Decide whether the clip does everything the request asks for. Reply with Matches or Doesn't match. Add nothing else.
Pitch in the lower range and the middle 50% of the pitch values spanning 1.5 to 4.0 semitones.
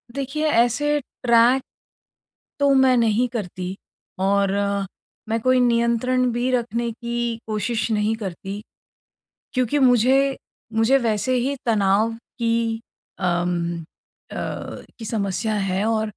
Doesn't match